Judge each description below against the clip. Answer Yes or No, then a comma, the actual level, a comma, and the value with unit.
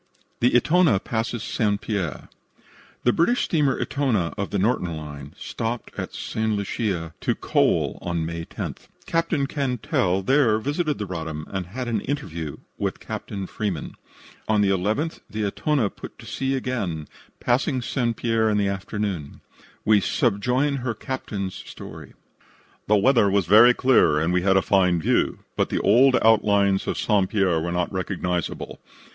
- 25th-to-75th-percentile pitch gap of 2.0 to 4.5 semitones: No, average, 5.2 semitones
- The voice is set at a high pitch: No, low, 105 Hz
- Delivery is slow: No, average, 155 wpm